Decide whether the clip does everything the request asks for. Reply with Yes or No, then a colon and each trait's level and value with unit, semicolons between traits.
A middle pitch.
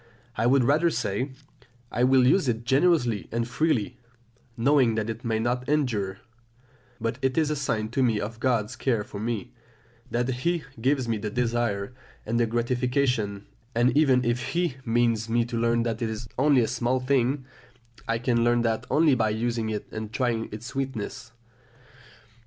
No: low, 120 Hz